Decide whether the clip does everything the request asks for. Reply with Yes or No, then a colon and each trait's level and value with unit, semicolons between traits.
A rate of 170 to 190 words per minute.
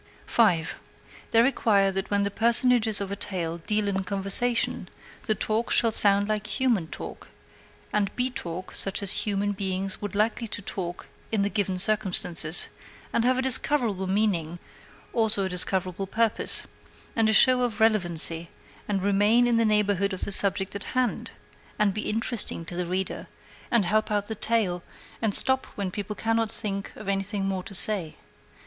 Yes: average, 175 wpm